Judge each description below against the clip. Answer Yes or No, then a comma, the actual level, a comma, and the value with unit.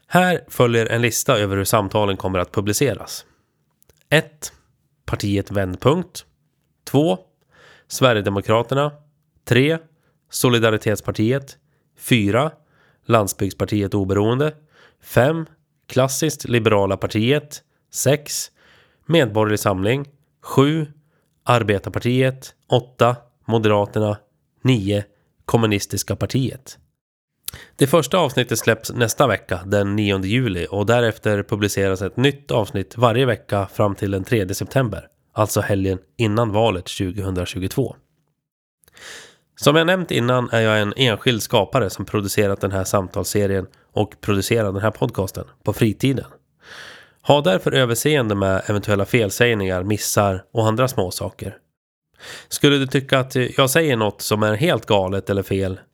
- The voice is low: Yes, low, 115 Hz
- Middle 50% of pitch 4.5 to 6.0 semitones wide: Yes, average, 4.9 semitones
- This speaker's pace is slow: Yes, slow, 115 wpm